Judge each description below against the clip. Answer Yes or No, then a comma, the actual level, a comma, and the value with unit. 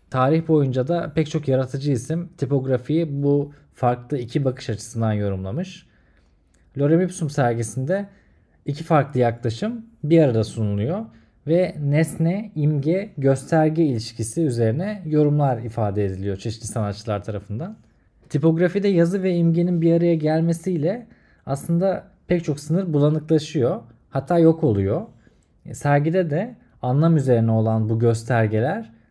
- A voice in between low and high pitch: Yes, medium, 145 Hz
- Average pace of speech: Yes, average, 120 wpm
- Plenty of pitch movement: Yes, wide, 6.3 semitones